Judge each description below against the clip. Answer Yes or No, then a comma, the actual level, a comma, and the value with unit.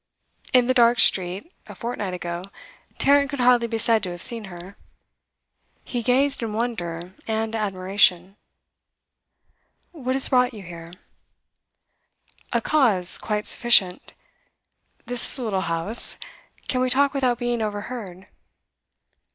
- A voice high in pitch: Yes, high, 225 Hz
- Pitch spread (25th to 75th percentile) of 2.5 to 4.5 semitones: No, average, 5.0 semitones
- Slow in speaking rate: Yes, slow, 130 wpm